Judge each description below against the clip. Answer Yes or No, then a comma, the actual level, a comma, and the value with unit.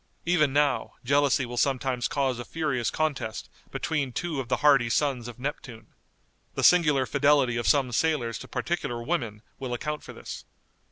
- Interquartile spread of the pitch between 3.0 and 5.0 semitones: Yes, average, 3.4 semitones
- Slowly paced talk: No, average, 165 wpm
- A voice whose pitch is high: No, low, 135 Hz